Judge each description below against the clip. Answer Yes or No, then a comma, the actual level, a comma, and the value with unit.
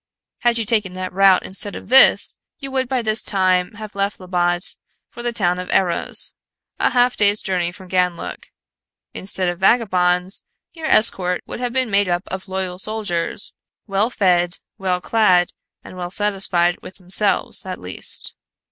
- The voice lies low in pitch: No, high, 190 Hz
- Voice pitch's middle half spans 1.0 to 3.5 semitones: Yes, average, 3.1 semitones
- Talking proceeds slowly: No, average, 165 wpm